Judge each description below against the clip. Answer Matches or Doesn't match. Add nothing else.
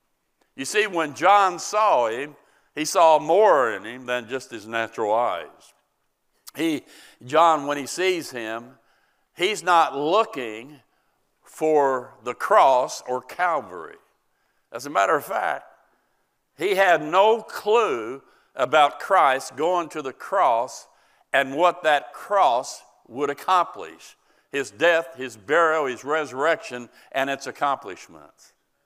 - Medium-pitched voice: Matches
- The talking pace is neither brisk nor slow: Doesn't match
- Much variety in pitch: Matches